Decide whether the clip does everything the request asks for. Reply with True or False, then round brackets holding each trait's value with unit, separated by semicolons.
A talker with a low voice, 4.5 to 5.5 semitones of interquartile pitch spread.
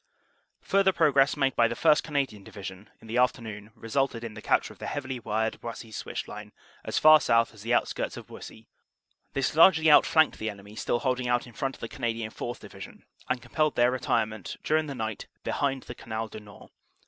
False (120 Hz; 3.8 semitones)